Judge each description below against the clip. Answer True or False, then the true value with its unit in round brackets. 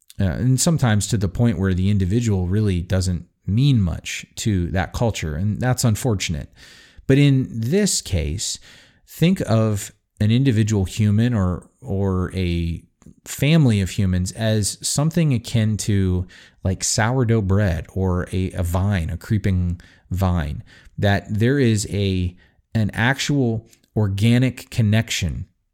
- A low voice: True (105 Hz)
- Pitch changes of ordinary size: True (4.2 semitones)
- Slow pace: True (130 wpm)